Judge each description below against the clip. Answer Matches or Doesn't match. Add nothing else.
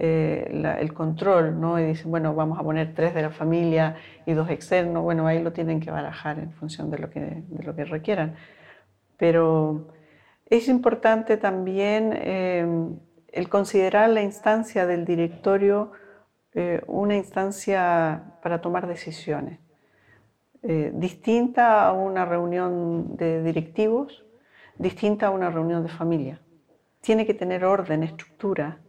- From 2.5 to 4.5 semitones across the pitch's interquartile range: Matches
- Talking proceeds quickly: Doesn't match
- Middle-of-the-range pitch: Matches